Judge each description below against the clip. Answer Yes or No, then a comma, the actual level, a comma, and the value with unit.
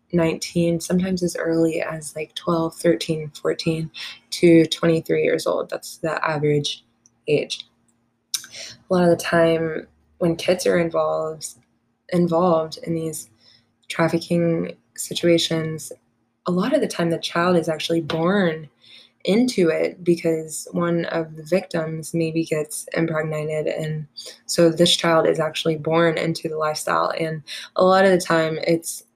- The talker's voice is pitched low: No, medium, 165 Hz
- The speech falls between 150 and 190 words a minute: No, average, 140 wpm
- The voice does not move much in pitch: Yes, narrow, 1.6 semitones